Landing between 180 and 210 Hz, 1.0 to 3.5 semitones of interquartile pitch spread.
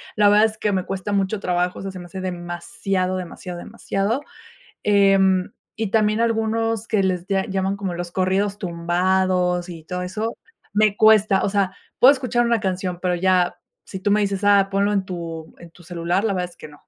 Yes: high, 190 Hz; narrow, 2.4 semitones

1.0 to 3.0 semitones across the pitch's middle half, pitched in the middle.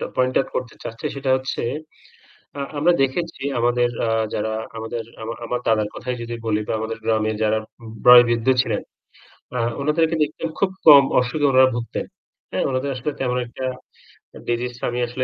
No: narrow, 2.6 semitones; low, 125 Hz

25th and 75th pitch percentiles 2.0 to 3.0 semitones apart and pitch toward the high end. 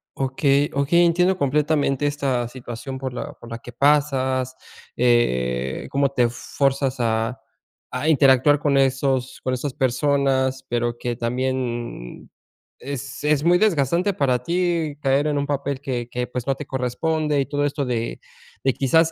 No: average, 2.7 semitones; low, 135 Hz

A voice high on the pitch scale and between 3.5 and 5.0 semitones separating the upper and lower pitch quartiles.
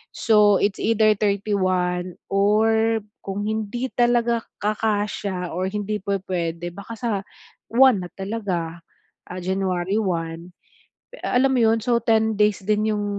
No: high, 205 Hz; average, 2.9 semitones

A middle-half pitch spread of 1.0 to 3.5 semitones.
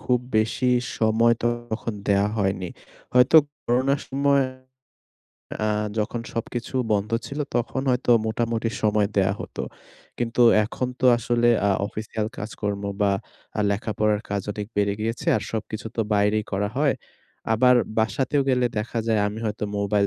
Yes: average, 2.9 semitones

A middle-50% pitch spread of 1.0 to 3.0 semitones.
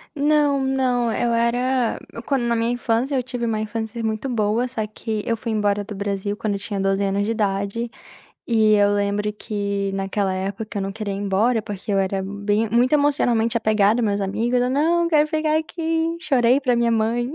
No: average, 3.5 semitones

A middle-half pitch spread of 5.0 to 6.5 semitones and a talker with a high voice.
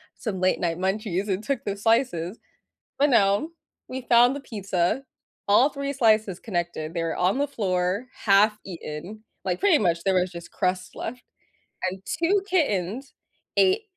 Yes: wide, 5.6 semitones; high, 200 Hz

